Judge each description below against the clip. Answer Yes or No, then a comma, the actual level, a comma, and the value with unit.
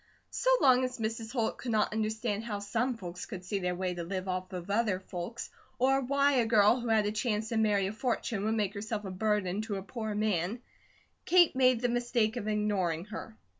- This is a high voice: Yes, high, 215 Hz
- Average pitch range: Yes, average, 3.1 semitones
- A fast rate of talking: Yes, fast, 215 wpm